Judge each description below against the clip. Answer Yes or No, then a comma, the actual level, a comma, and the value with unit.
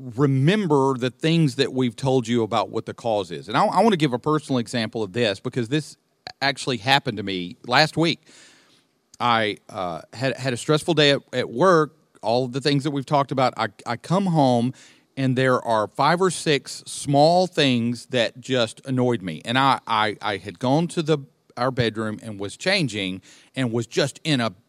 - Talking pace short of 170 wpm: No, average, 200 wpm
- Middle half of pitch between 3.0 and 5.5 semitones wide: Yes, average, 4.1 semitones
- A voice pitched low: Yes, low, 130 Hz